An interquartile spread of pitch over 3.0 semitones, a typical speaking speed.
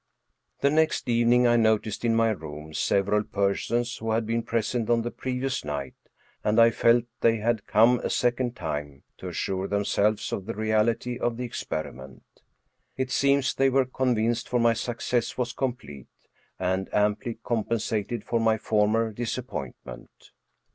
No: average, 2.7 semitones; average, 155 wpm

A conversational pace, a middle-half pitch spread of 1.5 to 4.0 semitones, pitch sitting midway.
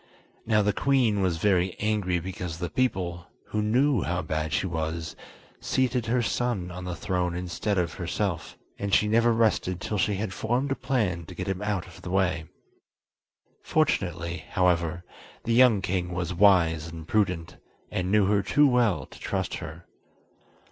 No: average, 170 wpm; average, 3.7 semitones; very low, 95 Hz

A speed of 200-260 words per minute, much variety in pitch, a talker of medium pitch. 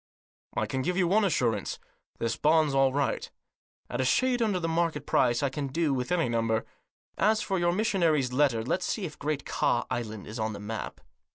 Yes: fast, 205 wpm; wide, 6.3 semitones; medium, 145 Hz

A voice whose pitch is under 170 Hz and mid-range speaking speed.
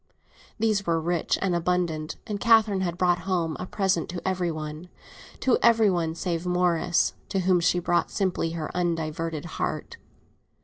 No: medium, 175 Hz; average, 160 wpm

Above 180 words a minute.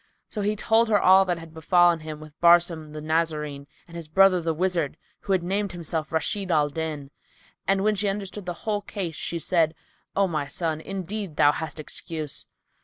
Yes: average, 190 wpm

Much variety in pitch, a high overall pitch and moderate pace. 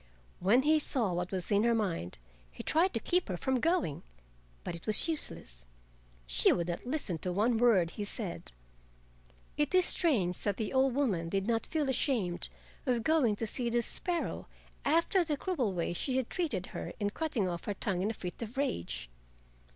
Yes: wide, 7.5 semitones; high, 225 Hz; average, 190 wpm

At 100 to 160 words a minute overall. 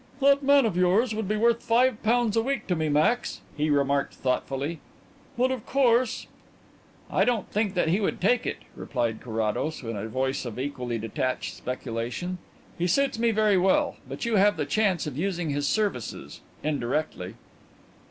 No: average, 175 wpm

